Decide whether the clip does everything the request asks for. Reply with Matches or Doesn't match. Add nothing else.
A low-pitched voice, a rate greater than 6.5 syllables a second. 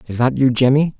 Doesn't match